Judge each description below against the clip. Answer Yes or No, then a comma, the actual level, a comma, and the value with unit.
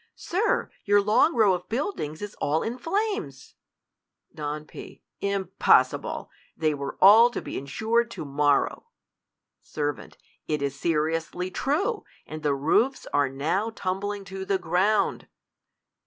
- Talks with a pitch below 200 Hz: Yes, high, 190 Hz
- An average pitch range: No, wide, 6.8 semitones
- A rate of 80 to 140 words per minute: Yes, slow, 135 wpm